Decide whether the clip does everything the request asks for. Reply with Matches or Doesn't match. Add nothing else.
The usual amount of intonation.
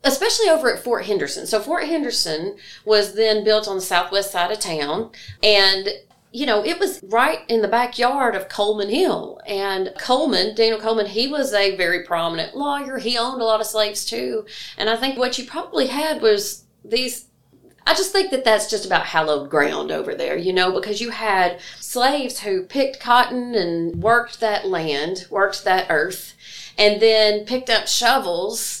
Matches